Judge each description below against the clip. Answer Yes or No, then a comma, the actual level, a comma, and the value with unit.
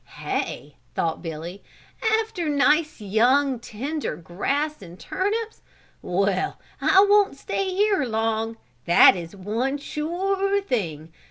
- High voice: Yes, very high, 265 Hz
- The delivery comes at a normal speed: No, slow, 110 wpm